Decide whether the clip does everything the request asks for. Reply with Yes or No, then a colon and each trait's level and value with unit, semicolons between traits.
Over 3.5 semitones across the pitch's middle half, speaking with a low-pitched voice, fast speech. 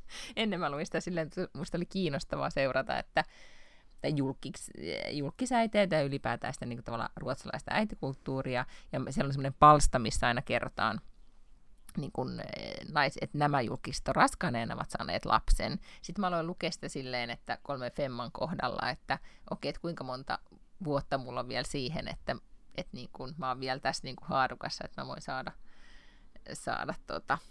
No: average, 4.4 semitones; medium, 145 Hz; fast, 165 wpm